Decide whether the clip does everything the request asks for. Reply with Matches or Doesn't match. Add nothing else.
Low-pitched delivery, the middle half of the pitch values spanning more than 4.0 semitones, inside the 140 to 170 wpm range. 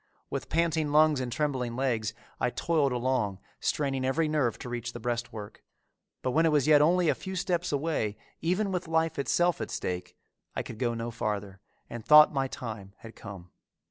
Doesn't match